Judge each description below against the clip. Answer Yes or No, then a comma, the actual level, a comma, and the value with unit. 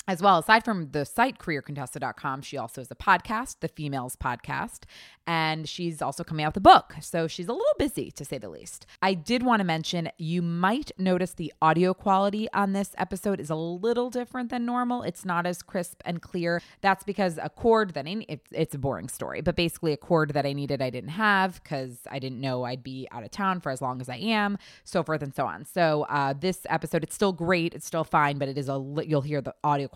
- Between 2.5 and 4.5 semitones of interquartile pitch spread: No, average, 5.2 semitones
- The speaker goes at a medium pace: No, fast, 240 wpm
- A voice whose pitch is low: No, medium, 170 Hz